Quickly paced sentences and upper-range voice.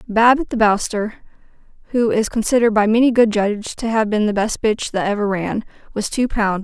Yes: fast, 210 wpm; high, 220 Hz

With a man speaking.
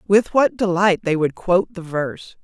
No: female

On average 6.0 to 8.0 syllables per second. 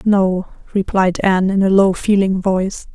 No: 4.7 syllables/s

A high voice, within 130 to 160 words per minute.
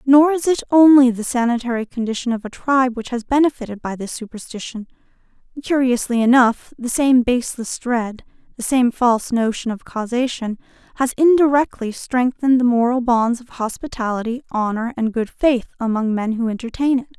Yes: high, 245 Hz; average, 155 wpm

